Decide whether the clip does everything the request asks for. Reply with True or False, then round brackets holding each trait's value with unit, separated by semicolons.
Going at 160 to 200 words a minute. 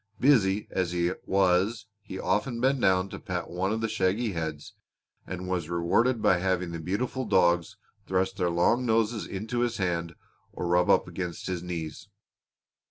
True (165 wpm)